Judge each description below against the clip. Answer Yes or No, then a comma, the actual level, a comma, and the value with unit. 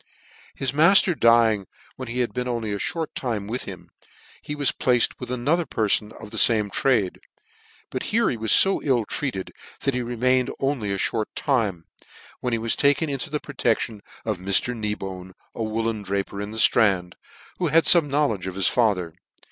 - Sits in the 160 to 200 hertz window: No, low, 115 Hz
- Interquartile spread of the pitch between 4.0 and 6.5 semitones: Yes, average, 4.5 semitones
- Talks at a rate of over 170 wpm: Yes, average, 190 wpm